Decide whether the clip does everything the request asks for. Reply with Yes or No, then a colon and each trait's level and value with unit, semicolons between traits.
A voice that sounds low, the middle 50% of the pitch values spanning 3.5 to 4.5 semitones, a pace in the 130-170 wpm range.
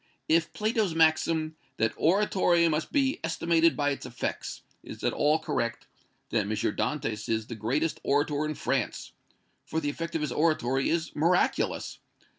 No: medium, 155 Hz; average, 4.2 semitones; average, 155 wpm